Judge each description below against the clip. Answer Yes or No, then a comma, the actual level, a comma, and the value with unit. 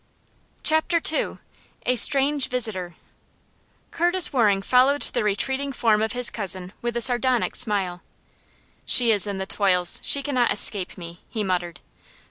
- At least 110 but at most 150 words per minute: Yes, average, 140 wpm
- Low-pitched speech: No, high, 225 Hz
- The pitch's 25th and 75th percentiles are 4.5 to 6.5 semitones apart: Yes, average, 5.2 semitones